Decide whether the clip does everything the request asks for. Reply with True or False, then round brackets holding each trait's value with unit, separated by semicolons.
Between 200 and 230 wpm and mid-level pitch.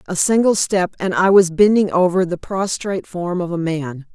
True (205 wpm; 180 Hz)